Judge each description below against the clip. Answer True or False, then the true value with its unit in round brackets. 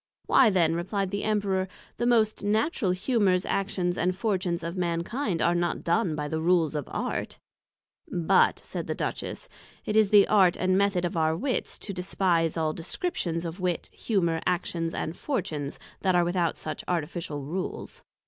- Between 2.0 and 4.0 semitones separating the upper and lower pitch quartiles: True (3.1 semitones)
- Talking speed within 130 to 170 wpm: True (165 wpm)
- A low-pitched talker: False (180 Hz)